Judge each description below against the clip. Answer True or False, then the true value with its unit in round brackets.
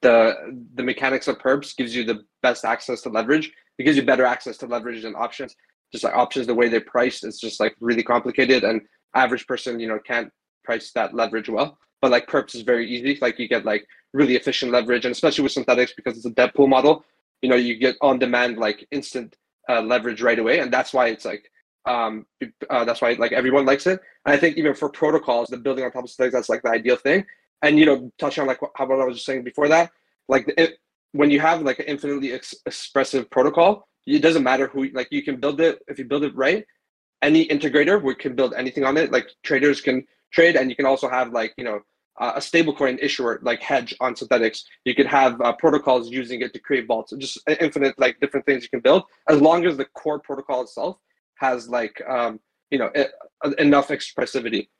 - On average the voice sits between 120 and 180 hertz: True (135 Hz)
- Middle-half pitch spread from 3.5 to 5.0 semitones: False (3.0 semitones)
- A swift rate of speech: True (230 wpm)